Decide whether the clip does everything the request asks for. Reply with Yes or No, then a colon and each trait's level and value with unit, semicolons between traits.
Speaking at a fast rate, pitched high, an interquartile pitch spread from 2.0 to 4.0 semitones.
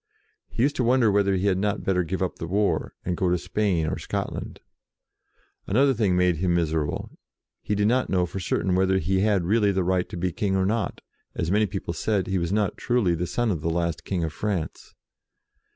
No: fast, 225 wpm; very low, 95 Hz; average, 2.9 semitones